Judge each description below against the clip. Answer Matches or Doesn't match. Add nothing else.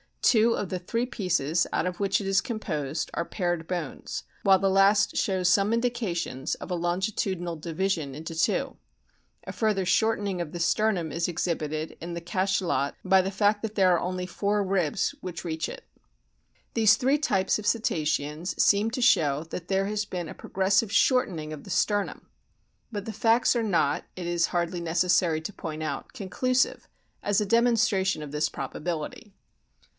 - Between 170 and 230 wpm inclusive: Matches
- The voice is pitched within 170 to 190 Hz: Matches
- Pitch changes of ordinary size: Matches